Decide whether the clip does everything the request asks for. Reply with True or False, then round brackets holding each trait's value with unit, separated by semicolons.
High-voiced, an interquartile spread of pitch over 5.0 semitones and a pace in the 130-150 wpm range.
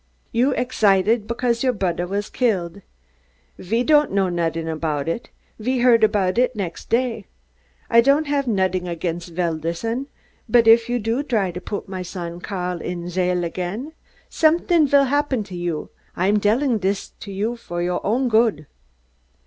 False (205 Hz; 5.4 semitones; 160 wpm)